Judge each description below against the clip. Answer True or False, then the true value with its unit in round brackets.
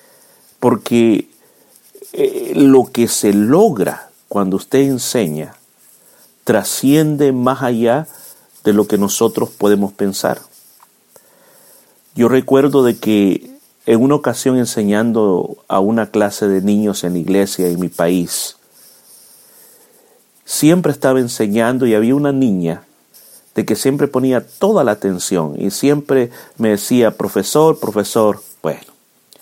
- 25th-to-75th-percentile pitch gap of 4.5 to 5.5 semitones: True (5.0 semitones)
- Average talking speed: False (115 wpm)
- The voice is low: True (115 Hz)